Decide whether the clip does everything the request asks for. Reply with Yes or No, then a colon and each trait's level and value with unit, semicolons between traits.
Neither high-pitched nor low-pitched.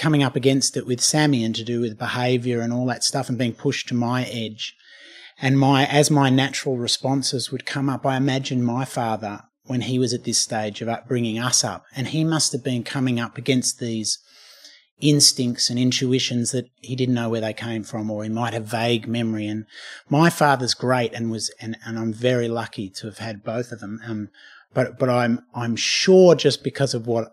No: low, 125 Hz